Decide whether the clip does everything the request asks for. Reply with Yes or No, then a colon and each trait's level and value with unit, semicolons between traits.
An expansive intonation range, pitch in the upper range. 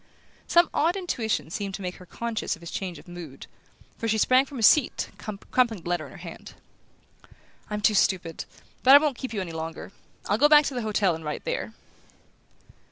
Yes: wide, 6.7 semitones; high, 210 Hz